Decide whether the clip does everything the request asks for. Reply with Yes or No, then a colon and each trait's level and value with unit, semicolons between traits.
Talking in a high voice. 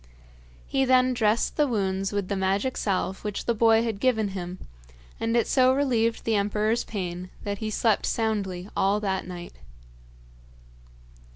Yes: high, 210 Hz